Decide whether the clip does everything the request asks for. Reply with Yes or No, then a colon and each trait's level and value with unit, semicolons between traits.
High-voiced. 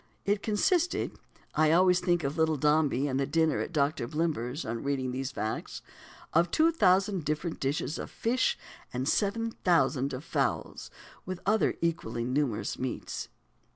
No: medium, 155 Hz